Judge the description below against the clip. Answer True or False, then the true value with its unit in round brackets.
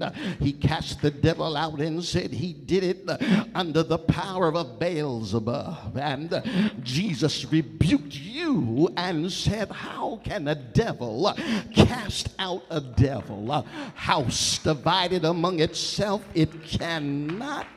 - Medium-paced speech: False (125 wpm)